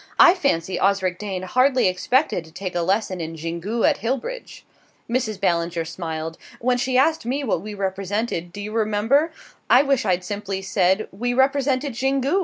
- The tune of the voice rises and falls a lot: Yes, wide, 5.9 semitones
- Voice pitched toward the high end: Yes, high, 210 Hz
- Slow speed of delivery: No, average, 170 wpm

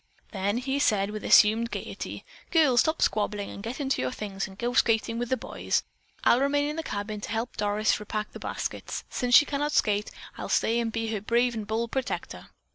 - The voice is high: Yes, high, 225 Hz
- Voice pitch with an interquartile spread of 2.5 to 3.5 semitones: Yes, average, 3.1 semitones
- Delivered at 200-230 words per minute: Yes, fast, 205 wpm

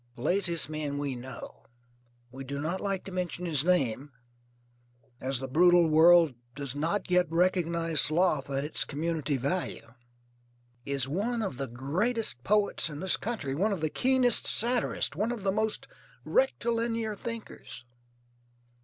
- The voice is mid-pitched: Yes, medium, 170 Hz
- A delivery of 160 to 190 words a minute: No, average, 145 wpm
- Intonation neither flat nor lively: No, wide, 6.1 semitones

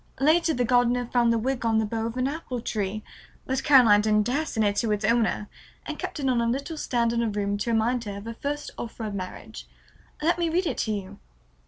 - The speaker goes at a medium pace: No, fast, 240 wpm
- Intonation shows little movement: No, average, 3.6 semitones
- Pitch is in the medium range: No, high, 235 Hz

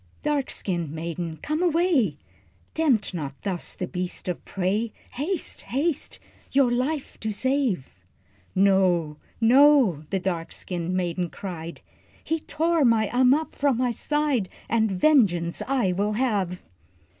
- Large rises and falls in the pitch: Yes, wide, 7.5 semitones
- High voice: Yes, high, 215 Hz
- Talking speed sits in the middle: No, slow, 130 wpm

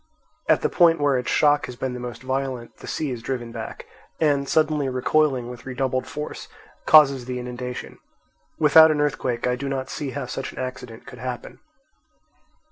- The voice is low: Yes, low, 130 Hz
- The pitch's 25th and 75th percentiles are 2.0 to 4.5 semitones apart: Yes, average, 2.7 semitones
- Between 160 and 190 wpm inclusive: Yes, average, 180 wpm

